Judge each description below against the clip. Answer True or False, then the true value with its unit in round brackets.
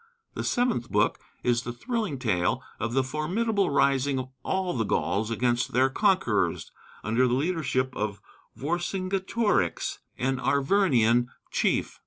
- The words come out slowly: True (130 wpm)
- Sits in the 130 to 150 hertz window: True (135 Hz)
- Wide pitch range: True (7.3 semitones)